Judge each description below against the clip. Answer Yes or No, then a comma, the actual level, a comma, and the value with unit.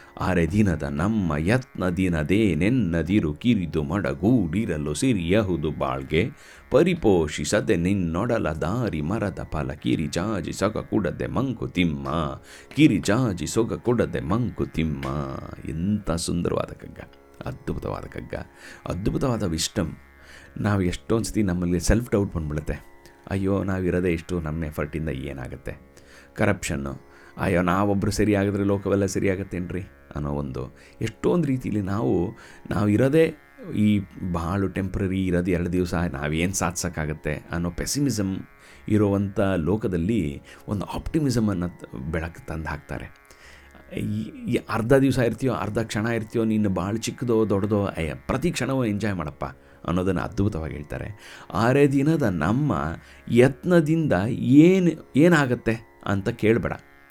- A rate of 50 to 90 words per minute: No, fast, 105 wpm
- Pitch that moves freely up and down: Yes, wide, 5.9 semitones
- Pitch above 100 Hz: No, very low, 90 Hz